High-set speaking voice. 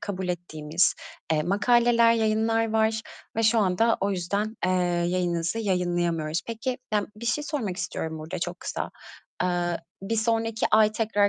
Yes: high, 205 Hz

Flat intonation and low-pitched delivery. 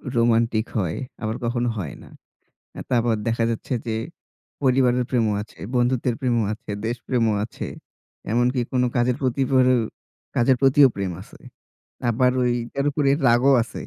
Yes: narrow, 1.9 semitones; low, 120 Hz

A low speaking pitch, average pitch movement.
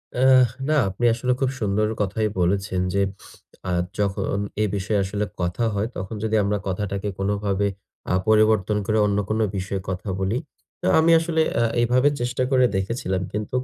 Yes: low, 105 Hz; average, 3.1 semitones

